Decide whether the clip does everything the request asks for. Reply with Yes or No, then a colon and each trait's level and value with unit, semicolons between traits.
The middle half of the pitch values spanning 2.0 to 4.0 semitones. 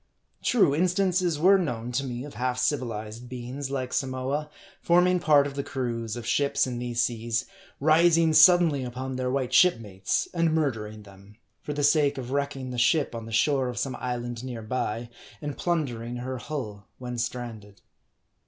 Yes: average, 3.7 semitones